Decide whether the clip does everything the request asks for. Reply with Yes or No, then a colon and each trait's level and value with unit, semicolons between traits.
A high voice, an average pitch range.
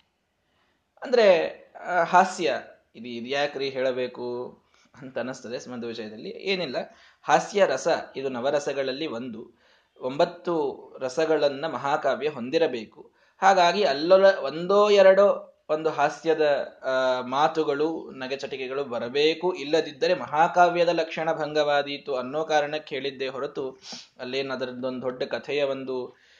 No: medium, 145 Hz; average, 3.9 semitones